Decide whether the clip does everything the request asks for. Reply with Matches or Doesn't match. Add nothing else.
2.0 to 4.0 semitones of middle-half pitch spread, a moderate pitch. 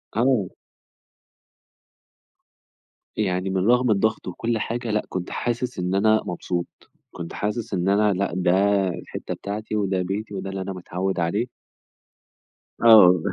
Doesn't match